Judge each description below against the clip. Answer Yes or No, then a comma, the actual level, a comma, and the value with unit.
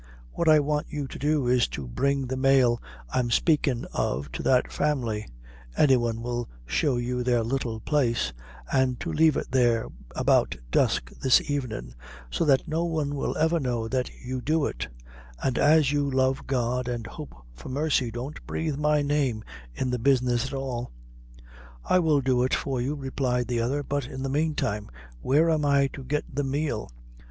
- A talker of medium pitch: No, low, 130 Hz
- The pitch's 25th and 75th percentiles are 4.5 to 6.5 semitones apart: No, average, 3.2 semitones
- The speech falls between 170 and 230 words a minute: Yes, average, 180 wpm